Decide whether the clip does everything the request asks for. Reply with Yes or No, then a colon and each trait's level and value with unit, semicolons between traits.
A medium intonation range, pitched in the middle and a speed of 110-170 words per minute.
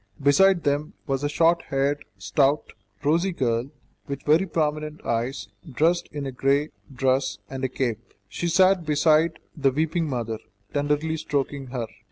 Yes: average, 3.1 semitones; medium, 145 Hz; average, 150 wpm